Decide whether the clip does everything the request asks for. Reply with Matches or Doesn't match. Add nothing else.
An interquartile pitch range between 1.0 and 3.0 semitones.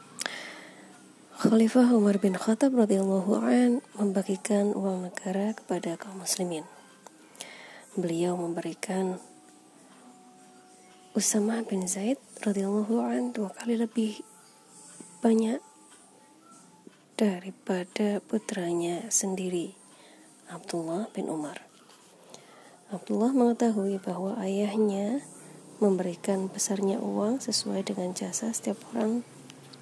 Doesn't match